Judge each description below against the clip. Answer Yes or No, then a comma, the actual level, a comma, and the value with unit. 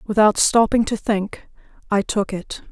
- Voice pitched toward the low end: No, high, 210 Hz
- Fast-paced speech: No, average, 155 wpm